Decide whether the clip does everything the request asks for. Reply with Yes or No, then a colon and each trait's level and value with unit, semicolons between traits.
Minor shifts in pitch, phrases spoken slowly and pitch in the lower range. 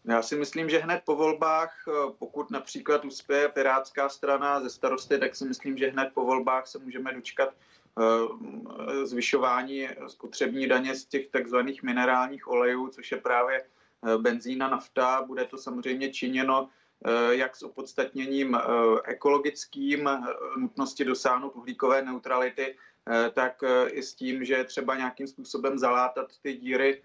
No: narrow, 1.5 semitones; average, 135 wpm; low, 130 Hz